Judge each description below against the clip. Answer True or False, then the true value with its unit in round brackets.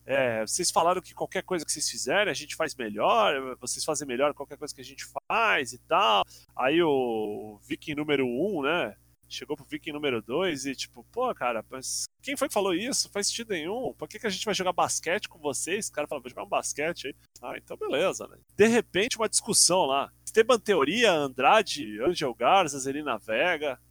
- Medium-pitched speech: True (150 Hz)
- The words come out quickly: True (210 wpm)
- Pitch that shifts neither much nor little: False (7.7 semitones)